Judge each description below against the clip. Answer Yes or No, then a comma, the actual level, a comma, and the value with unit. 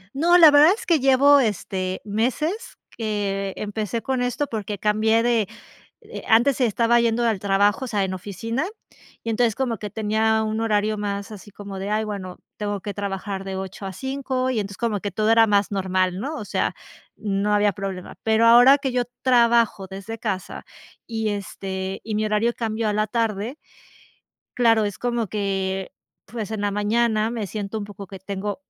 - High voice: Yes, high, 215 Hz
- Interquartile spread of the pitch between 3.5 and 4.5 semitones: No, average, 2.8 semitones